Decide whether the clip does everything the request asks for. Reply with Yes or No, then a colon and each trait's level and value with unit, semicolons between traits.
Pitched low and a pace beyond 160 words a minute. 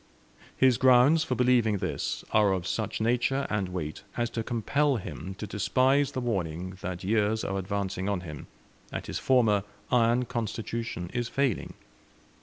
No: low, 110 Hz; average, 155 wpm